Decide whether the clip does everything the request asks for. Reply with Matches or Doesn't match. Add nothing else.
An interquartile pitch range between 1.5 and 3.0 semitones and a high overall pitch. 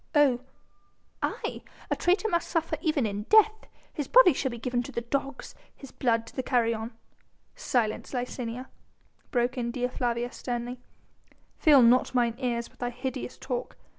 Matches